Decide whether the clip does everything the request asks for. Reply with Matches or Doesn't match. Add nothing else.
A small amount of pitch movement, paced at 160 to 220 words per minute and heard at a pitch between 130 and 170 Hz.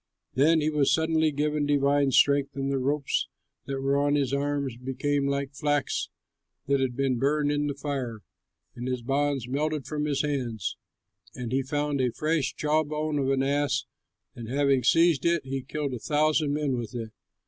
Matches